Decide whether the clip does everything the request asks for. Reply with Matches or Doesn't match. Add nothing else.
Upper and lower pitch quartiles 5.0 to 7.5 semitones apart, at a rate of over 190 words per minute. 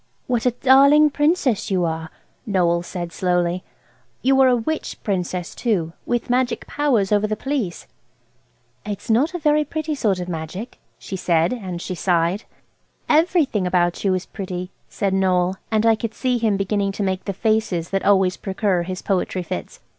Doesn't match